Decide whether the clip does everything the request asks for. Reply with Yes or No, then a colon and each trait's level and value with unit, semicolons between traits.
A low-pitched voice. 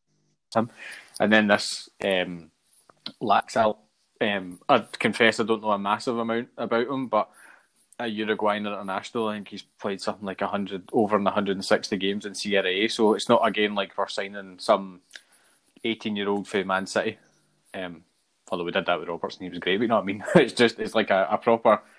Yes: low, 100 Hz